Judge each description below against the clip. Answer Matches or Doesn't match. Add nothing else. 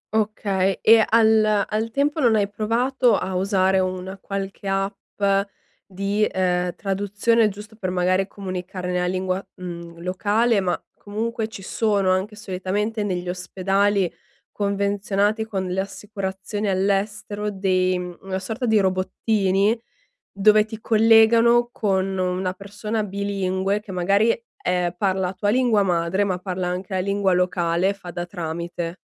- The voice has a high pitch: Matches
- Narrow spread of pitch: Matches